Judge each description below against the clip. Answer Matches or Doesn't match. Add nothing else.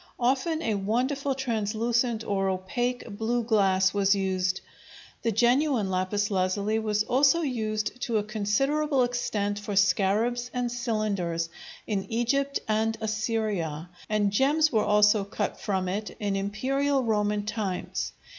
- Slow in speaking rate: Matches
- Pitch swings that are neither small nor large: Matches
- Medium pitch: Doesn't match